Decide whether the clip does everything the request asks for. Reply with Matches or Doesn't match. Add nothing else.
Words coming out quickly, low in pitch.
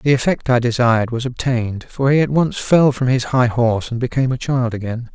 Matches